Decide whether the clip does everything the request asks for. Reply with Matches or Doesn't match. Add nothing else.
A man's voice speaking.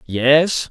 Matches